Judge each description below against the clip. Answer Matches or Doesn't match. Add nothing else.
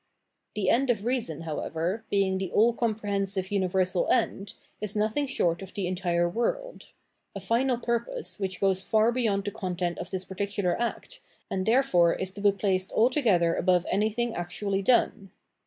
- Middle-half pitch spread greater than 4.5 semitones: Doesn't match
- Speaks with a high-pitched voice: Matches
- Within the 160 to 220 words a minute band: Matches